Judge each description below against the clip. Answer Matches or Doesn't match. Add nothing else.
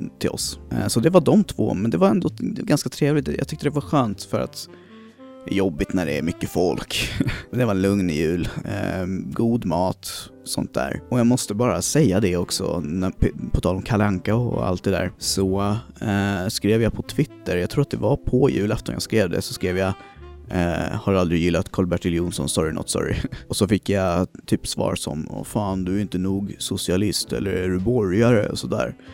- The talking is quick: Matches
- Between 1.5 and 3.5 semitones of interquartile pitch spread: Doesn't match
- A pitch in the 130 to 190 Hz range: Doesn't match